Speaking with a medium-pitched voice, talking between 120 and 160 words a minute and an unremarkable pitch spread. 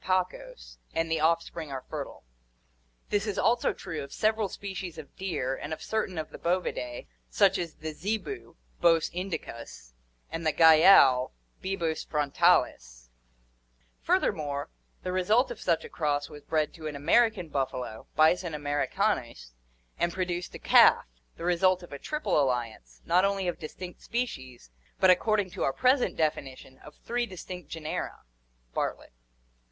Yes: medium, 165 Hz; average, 150 wpm; average, 4.6 semitones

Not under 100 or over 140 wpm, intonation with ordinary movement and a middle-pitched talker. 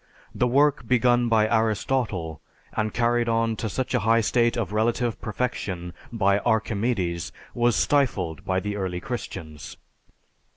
No: slow, 135 wpm; average, 3.5 semitones; low, 110 Hz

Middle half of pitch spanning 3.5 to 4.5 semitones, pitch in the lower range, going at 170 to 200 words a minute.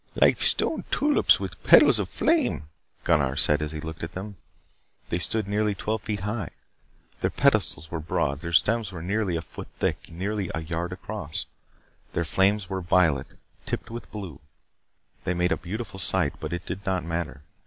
Yes: average, 4.0 semitones; very low, 90 Hz; average, 175 wpm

